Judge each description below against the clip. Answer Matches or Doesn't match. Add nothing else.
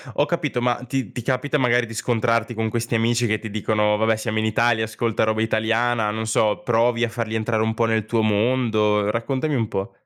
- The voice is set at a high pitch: Doesn't match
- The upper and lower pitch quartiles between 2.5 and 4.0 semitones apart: Doesn't match